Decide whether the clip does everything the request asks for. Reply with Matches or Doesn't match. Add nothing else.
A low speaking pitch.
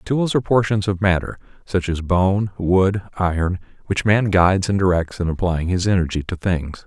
Matches